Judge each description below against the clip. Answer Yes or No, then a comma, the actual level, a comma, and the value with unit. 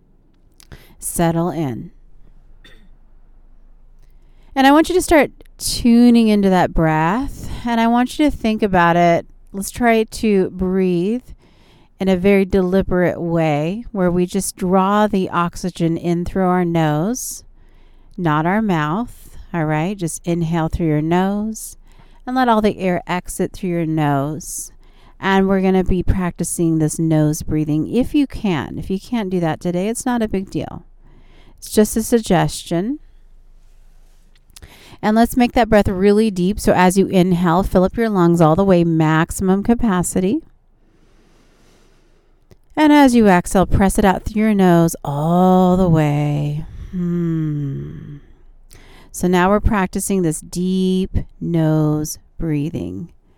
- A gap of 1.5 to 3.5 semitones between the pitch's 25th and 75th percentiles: No, average, 4.2 semitones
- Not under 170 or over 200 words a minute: No, average, 145 wpm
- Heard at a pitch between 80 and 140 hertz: No, medium, 185 Hz